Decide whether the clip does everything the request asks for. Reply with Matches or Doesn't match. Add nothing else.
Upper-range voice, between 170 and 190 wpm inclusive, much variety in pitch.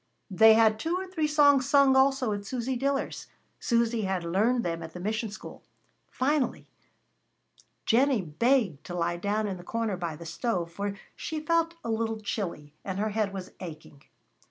Matches